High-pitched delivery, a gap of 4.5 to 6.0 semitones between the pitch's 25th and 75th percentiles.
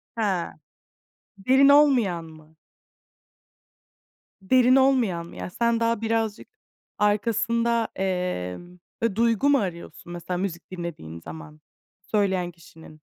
Yes: high, 195 Hz; average, 5.2 semitones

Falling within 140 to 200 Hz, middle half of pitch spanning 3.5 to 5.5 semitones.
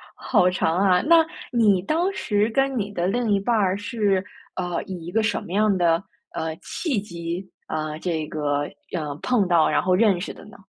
Yes: high, 190 Hz; average, 4.1 semitones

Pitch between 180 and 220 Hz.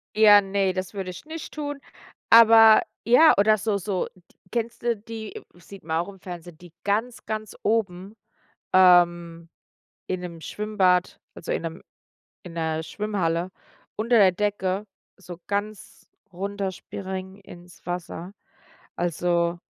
Yes: high, 190 Hz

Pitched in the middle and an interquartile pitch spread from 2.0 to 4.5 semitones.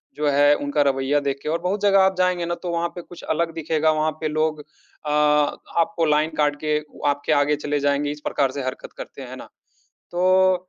Yes: medium, 155 Hz; average, 2.9 semitones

